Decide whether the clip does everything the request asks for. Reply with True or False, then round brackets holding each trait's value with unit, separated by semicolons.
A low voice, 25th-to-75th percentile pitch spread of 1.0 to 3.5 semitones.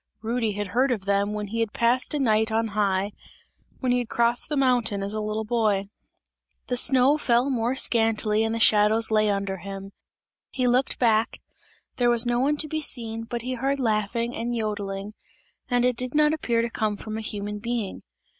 False (225 Hz; 2.8 semitones)